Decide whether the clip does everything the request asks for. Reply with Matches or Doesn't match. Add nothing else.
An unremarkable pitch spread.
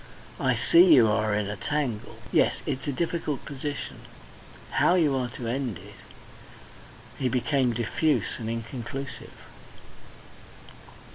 Matches